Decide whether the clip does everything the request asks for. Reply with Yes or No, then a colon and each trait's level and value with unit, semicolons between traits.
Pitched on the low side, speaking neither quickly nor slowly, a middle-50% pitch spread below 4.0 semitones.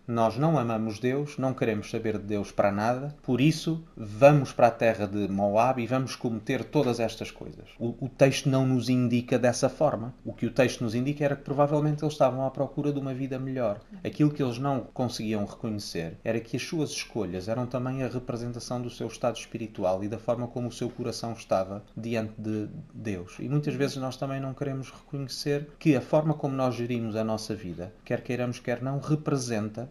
No: low, 125 Hz; fast, 205 wpm; average, 3.6 semitones